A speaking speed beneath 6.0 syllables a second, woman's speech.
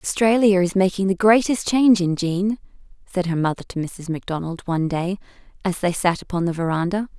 Yes: 5.8 syllables/s; female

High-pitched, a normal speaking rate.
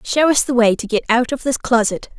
No: high, 240 Hz; fast, 275 wpm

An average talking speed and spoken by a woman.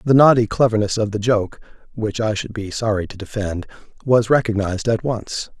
No: average, 180 wpm; male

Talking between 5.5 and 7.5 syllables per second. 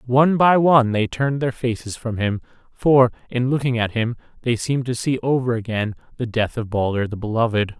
Yes: 5.6 syllables/s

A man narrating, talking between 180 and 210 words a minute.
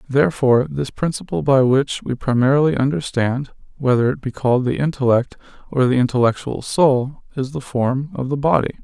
No: male; average, 165 wpm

